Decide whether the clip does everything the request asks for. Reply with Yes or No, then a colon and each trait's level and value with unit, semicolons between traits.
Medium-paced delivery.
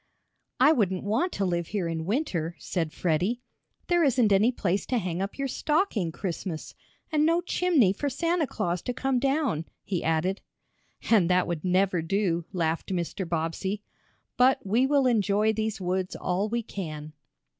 Yes: average, 165 wpm